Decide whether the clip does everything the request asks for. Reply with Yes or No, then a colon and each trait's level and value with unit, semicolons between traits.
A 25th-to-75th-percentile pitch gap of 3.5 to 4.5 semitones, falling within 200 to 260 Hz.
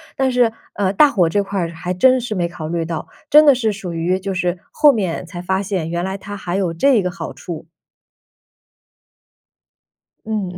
No: average, 3.9 semitones; high, 190 Hz